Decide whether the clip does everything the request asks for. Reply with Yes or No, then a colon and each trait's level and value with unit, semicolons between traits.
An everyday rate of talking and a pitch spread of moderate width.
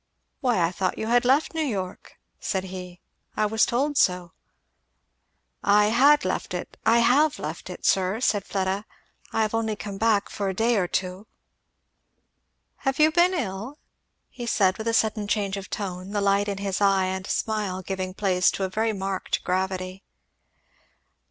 Yes: average, 175 wpm; average, 3.3 semitones